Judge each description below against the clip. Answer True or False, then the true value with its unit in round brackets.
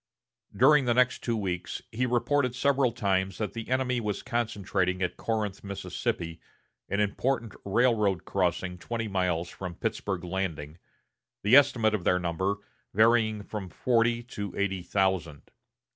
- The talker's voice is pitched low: True (105 Hz)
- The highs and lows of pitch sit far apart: False (4.1 semitones)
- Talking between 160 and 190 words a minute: False (140 wpm)